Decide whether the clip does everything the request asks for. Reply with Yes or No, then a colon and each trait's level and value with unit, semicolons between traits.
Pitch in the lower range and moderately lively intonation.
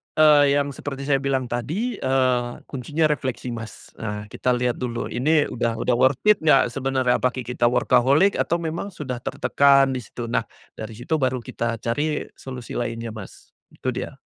Yes: low, 130 Hz; average, 3.1 semitones